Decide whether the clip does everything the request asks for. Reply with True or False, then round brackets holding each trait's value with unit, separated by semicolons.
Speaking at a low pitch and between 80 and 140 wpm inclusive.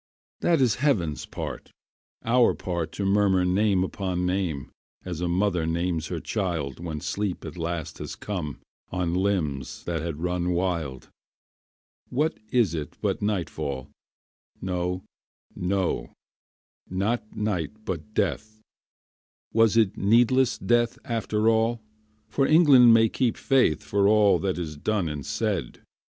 True (95 Hz; 135 wpm)